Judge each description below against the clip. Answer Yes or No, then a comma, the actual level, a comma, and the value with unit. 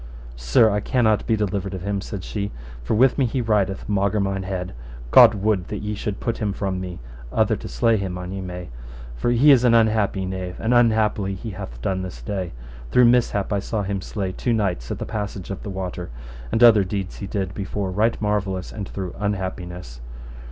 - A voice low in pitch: Yes, low, 100 Hz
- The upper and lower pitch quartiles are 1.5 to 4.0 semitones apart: Yes, narrow, 2.6 semitones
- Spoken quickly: Yes, fast, 210 wpm